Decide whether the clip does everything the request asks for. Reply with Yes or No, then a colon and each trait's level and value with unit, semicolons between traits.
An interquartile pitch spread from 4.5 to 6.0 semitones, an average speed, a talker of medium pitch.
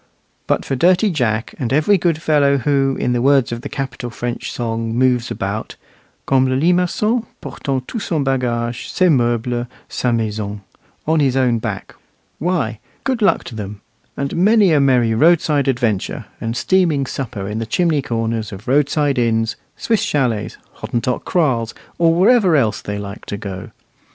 No: average, 5.2 semitones; average, 165 wpm; low, 130 Hz